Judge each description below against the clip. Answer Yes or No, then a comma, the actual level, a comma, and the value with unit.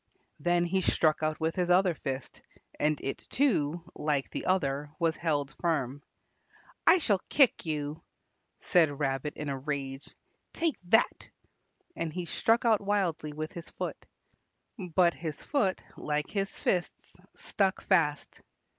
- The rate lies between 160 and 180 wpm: No, average, 140 wpm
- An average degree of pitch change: Yes, average, 4.1 semitones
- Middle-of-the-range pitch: Yes, medium, 165 Hz